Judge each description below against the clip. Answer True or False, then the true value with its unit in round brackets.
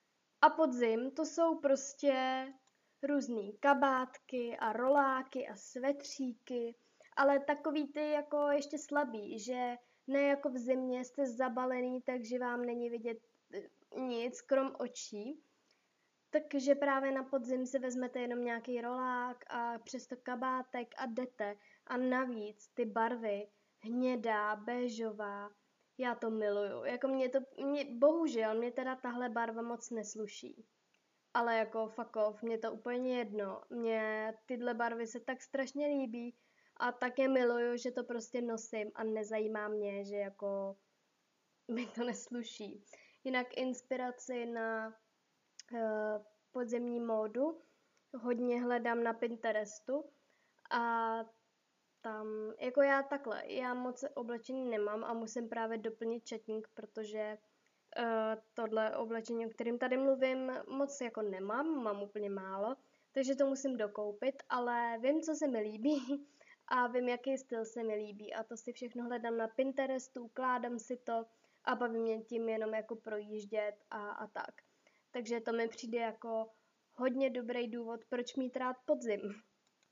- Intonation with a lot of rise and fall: False (2.8 semitones)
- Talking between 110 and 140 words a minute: True (135 wpm)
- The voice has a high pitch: True (240 Hz)